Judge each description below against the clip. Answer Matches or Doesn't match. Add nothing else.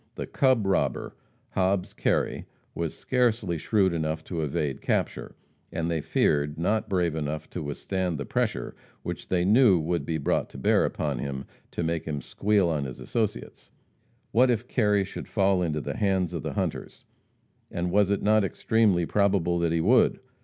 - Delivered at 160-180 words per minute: Matches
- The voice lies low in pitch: Matches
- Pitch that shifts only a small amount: Doesn't match